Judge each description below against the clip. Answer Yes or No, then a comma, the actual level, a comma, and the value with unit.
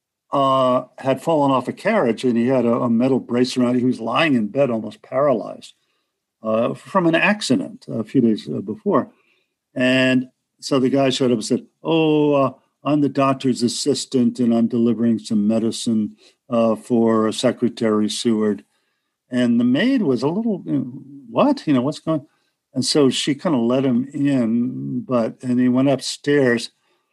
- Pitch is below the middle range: Yes, low, 125 Hz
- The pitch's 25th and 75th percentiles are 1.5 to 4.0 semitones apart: Yes, average, 3.1 semitones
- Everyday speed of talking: Yes, average, 175 wpm